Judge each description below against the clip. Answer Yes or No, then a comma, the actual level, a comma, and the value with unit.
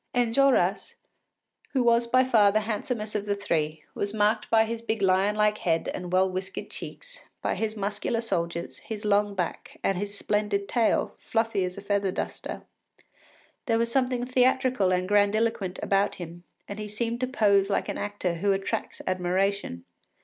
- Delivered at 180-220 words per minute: No, average, 170 wpm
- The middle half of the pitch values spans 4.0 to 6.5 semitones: No, average, 3.0 semitones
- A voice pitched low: No, high, 205 Hz